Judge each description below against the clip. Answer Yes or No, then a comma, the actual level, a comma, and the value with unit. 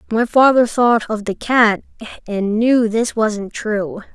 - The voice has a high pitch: Yes, high, 220 Hz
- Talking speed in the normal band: Yes, average, 160 wpm